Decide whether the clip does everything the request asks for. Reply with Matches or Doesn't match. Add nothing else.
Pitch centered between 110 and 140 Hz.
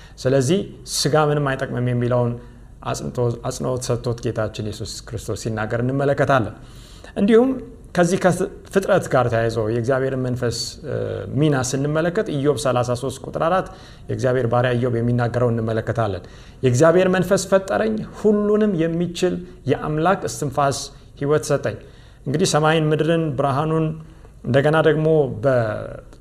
Matches